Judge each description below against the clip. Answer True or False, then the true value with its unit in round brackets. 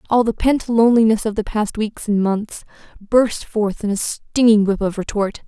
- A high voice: True (215 Hz)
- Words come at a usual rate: True (195 wpm)